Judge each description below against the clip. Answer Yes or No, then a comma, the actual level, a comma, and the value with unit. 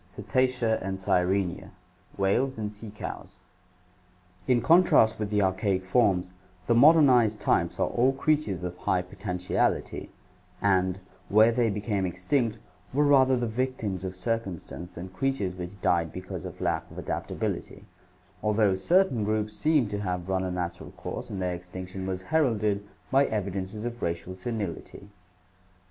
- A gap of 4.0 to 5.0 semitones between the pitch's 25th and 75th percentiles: Yes, average, 4.4 semitones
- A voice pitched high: No, low, 100 Hz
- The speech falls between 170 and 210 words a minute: No, average, 145 wpm